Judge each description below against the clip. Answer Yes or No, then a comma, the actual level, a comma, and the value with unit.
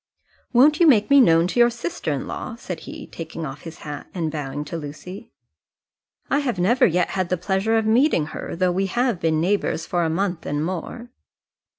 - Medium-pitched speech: Yes, medium, 180 Hz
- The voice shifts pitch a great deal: Yes, wide, 6.2 semitones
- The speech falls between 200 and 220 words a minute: Yes, fast, 205 wpm